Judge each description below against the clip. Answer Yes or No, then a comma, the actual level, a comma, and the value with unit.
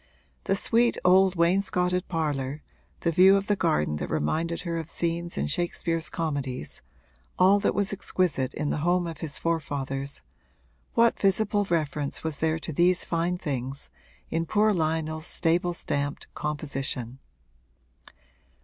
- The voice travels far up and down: No, average, 3.9 semitones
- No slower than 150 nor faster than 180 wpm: No, average, 140 wpm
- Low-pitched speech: No, medium, 165 Hz